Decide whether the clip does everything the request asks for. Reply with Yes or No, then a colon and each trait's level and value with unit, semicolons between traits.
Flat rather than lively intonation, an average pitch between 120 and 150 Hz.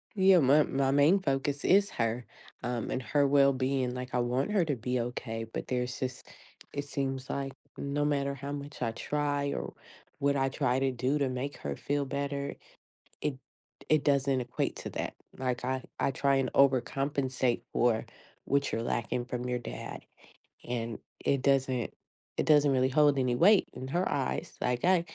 Yes: narrow, 2.1 semitones; low, 135 Hz